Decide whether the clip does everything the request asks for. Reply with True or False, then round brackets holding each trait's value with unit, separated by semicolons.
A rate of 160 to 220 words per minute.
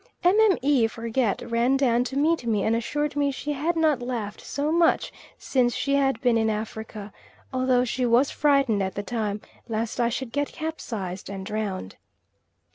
True (170 wpm)